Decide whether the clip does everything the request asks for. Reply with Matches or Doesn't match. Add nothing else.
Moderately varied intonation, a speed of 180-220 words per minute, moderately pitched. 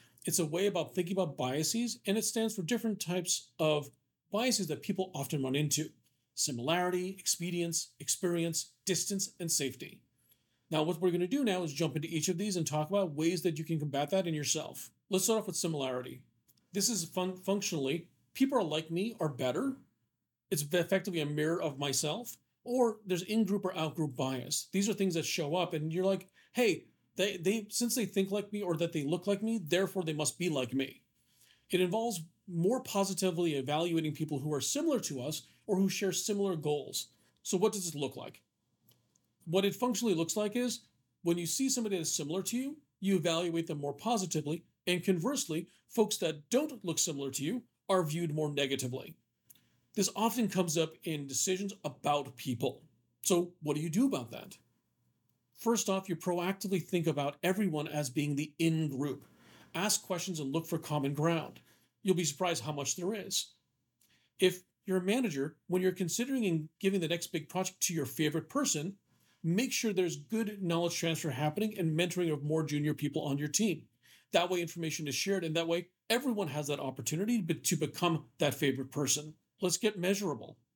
Matches